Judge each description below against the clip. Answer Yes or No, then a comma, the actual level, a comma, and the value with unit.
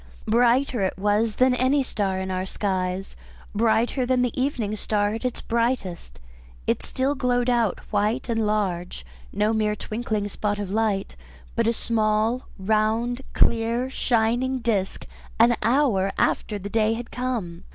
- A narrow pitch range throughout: No, average, 3.0 semitones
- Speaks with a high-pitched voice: Yes, high, 220 Hz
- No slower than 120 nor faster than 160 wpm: Yes, average, 150 wpm